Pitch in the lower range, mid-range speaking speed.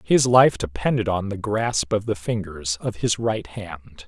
Yes: low, 100 Hz; average, 190 wpm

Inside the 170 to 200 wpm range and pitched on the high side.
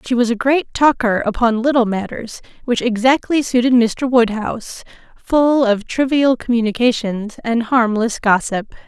No: slow, 135 wpm; high, 240 Hz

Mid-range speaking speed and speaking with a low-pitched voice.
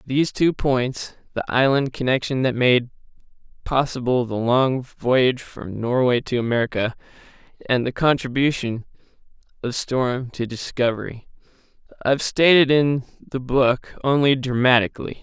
No: slow, 115 wpm; low, 130 Hz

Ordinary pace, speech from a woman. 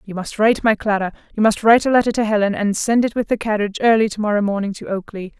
No: fast, 255 wpm; female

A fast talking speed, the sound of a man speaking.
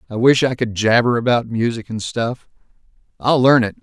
No: average, 190 wpm; male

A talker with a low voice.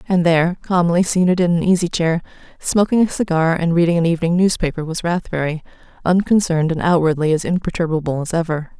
No: medium, 170 Hz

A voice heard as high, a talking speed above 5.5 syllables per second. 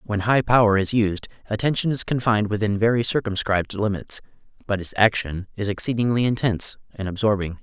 No: low, 105 Hz; 5.9 syllables/s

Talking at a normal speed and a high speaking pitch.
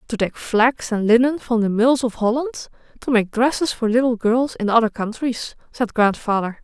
Yes: average, 190 wpm; high, 235 Hz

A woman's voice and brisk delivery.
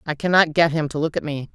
Yes: female; fast, 310 wpm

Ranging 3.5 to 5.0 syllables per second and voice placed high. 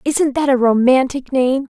Yes: 4.4 syllables/s; very high, 260 Hz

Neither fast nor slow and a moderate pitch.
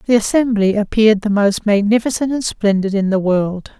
No: average, 175 wpm; high, 210 Hz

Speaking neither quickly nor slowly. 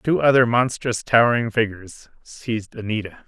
No: slow, 130 wpm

